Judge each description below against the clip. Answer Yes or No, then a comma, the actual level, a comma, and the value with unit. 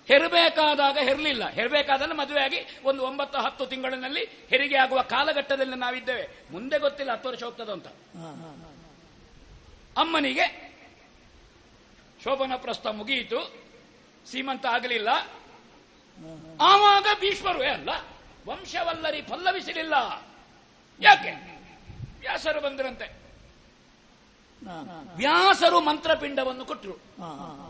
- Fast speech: No, average, 75 wpm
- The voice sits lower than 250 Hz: No, very high, 280 Hz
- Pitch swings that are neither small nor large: Yes, average, 3.5 semitones